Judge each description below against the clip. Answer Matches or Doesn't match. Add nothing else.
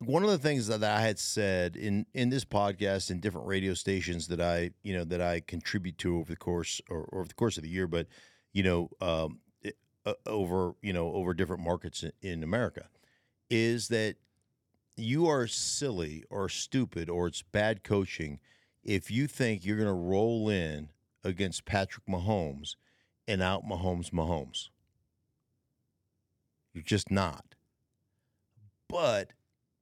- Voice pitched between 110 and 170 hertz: Doesn't match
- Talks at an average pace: Matches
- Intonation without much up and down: Doesn't match